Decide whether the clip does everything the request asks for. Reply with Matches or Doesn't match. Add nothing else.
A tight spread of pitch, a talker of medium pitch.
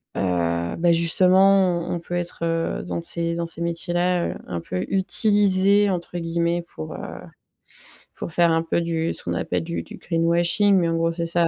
Matches